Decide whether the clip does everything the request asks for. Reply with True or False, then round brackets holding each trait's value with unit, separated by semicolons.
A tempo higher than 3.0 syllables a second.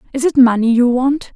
True (5.6 syllables/s)